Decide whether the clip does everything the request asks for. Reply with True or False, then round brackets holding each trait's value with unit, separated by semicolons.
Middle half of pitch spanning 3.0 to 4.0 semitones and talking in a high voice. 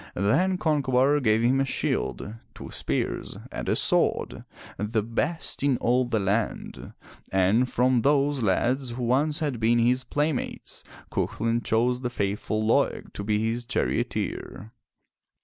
False (3.5 semitones; 120 Hz)